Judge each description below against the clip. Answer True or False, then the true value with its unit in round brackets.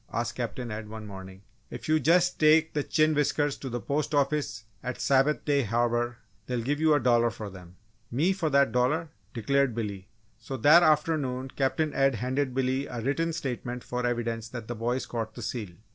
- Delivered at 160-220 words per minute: True (190 wpm)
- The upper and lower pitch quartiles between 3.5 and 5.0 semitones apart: True (3.9 semitones)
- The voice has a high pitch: False (130 Hz)